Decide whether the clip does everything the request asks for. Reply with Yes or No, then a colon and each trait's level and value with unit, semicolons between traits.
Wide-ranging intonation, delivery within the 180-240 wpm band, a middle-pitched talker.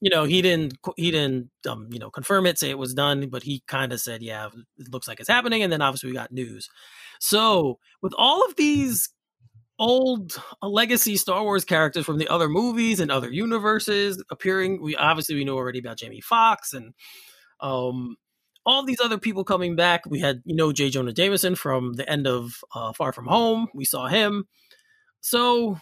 Yes: wide, 8.4 semitones; average, 200 wpm; medium, 160 Hz